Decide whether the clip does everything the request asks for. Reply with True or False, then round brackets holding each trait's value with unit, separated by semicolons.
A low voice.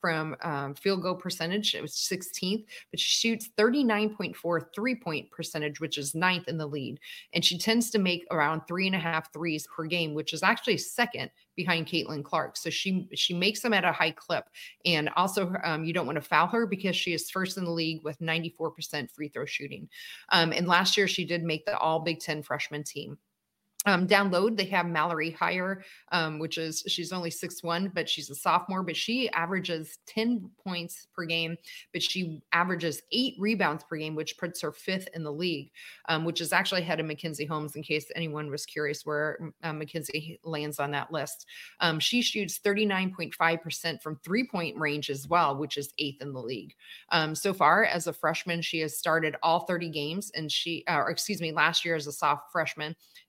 False (170 Hz)